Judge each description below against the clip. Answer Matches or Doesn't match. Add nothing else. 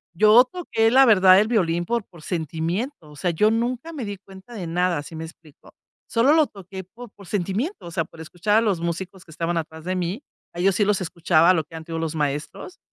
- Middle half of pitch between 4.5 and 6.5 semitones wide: Matches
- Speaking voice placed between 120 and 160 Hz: Doesn't match